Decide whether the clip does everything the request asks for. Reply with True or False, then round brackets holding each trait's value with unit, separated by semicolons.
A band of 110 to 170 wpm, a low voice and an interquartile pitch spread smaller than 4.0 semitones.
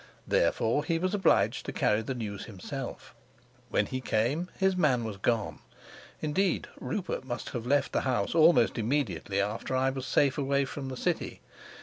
False (165 wpm; 130 Hz; 5.2 semitones)